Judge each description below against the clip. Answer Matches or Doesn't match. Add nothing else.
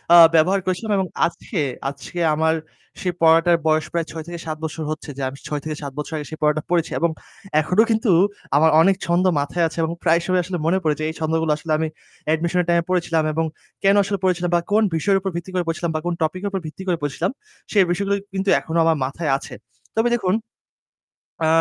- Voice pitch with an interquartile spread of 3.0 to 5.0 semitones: Doesn't match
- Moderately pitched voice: Matches